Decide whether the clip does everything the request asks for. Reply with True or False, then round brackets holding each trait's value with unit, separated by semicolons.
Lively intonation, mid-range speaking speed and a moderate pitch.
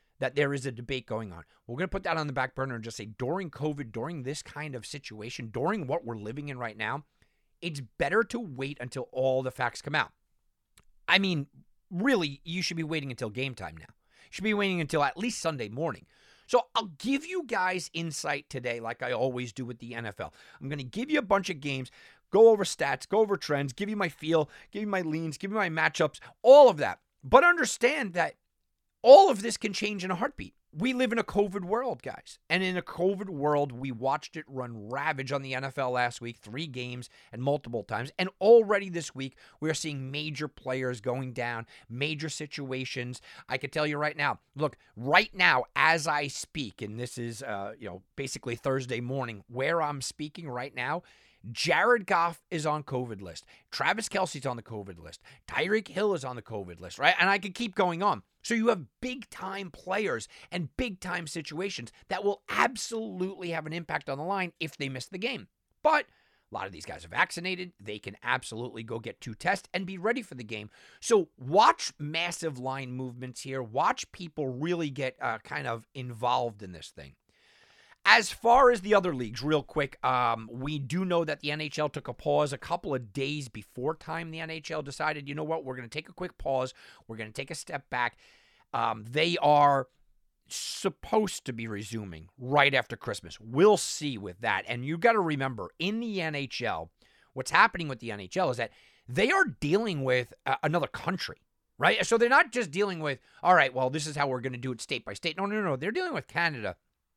False (6.6 semitones; 215 wpm; 145 Hz)